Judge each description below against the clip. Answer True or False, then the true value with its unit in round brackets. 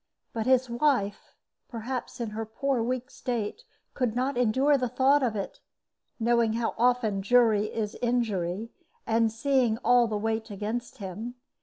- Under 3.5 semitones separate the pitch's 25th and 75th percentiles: True (2.4 semitones)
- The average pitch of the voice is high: True (235 Hz)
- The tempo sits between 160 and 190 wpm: False (150 wpm)